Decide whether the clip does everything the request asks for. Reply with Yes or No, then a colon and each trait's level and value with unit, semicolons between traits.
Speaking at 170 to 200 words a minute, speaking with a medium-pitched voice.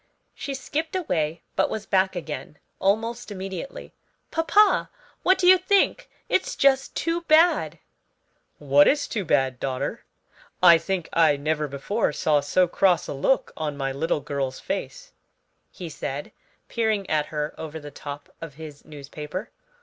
No: average, 150 wpm; medium, 165 Hz